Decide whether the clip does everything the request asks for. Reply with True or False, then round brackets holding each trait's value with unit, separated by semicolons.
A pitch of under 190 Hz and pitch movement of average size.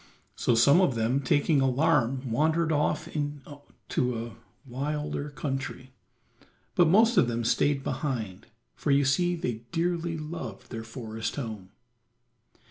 True (140 Hz; 4.4 semitones)